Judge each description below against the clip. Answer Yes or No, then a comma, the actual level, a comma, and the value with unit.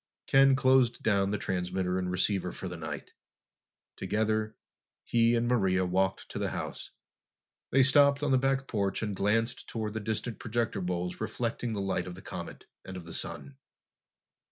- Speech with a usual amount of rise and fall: Yes, average, 4.4 semitones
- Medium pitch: No, low, 105 Hz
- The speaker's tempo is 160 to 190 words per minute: Yes, average, 170 wpm